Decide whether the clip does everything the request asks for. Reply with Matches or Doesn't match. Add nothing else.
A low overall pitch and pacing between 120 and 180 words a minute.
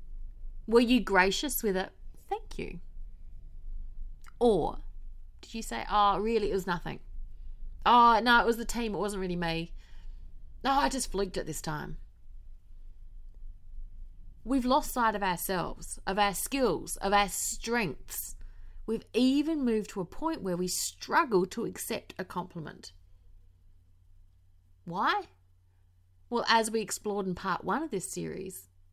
Doesn't match